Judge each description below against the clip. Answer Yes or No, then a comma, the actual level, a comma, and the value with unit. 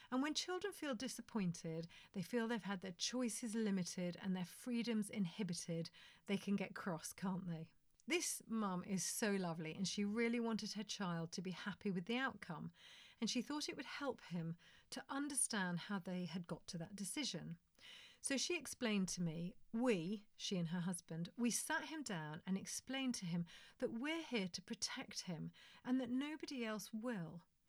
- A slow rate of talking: No, average, 180 wpm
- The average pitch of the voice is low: No, high, 205 Hz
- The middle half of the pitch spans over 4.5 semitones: Yes, average, 5.2 semitones